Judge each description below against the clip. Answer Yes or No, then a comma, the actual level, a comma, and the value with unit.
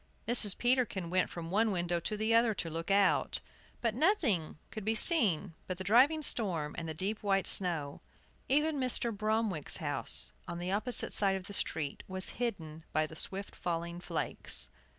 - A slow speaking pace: No, average, 175 wpm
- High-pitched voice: Yes, high, 195 Hz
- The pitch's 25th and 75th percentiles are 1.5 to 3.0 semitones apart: No, average, 5.0 semitones